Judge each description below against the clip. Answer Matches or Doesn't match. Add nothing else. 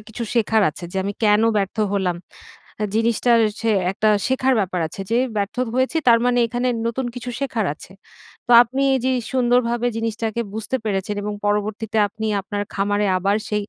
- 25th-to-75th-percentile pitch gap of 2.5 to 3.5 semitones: Matches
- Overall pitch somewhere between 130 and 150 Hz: Doesn't match